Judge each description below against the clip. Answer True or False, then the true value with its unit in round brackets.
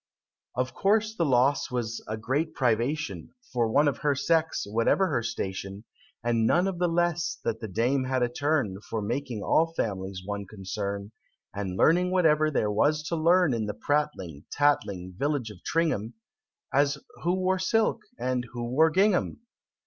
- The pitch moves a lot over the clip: True (6.6 semitones)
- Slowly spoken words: False (165 wpm)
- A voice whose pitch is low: True (130 Hz)